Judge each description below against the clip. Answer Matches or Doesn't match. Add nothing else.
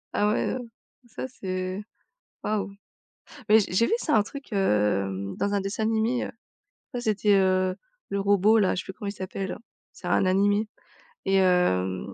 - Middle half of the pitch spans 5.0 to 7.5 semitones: Doesn't match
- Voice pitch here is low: Doesn't match